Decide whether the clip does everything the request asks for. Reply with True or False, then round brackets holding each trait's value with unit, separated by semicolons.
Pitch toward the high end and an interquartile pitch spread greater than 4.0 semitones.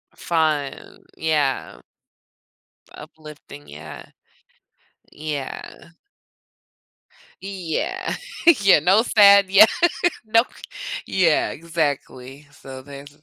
False (160 Hz; 5.5 semitones)